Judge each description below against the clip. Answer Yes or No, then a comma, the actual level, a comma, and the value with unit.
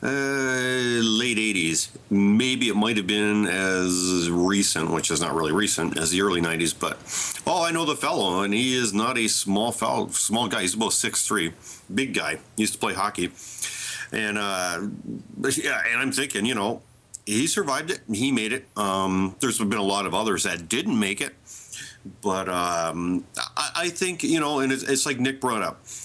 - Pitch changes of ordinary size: No, wide, 5.8 semitones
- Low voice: Yes, low, 105 Hz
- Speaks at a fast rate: No, average, 195 wpm